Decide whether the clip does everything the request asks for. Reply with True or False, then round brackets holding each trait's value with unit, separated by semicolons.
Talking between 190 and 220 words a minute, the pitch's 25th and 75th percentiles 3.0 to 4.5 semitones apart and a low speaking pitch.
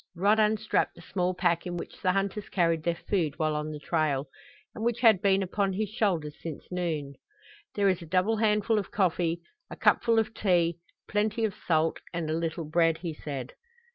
False (195 wpm; 4.1 semitones; 180 Hz)